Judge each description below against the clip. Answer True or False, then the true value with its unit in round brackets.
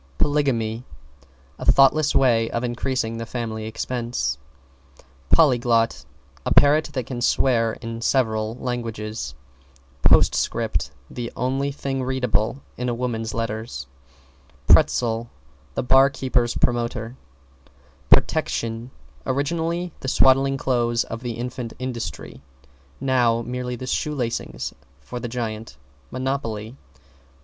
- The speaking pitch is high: False (120 Hz)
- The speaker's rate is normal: False (110 wpm)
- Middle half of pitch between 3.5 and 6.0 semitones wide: False (2.4 semitones)